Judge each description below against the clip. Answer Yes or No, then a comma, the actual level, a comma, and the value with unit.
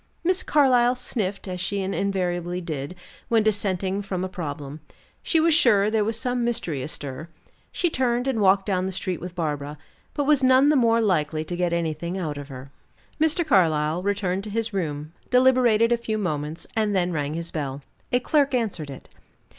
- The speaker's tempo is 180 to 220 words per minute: Yes, average, 185 wpm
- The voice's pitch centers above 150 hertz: Yes, high, 190 Hz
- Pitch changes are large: Yes, wide, 6.5 semitones